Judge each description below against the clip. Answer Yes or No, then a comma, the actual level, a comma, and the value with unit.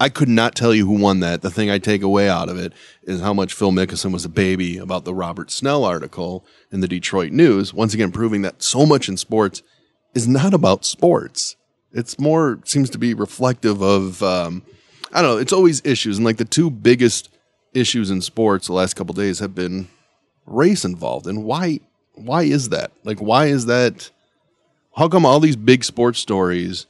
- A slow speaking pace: No, fast, 205 wpm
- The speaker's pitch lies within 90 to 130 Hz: Yes, low, 105 Hz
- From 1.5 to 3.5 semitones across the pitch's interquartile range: No, average, 5.0 semitones